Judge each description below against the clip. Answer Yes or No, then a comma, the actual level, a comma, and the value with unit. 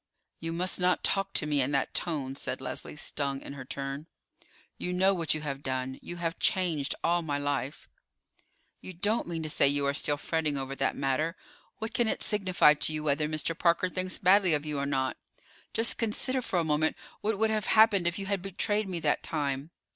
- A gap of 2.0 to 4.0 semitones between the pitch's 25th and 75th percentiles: No, average, 4.6 semitones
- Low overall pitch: No, medium, 160 Hz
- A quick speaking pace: Yes, fast, 210 wpm